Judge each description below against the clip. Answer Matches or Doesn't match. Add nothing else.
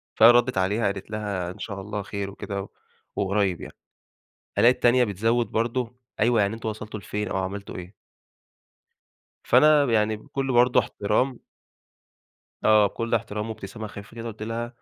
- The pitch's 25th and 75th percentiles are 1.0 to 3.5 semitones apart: Matches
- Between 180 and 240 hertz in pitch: Doesn't match